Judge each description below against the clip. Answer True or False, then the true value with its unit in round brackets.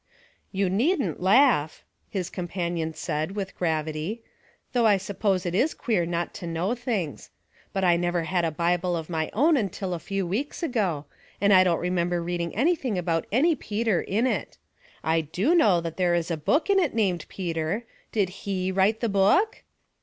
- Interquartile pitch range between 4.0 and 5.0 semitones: True (4.3 semitones)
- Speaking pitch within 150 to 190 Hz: True (185 Hz)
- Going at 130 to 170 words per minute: False (185 wpm)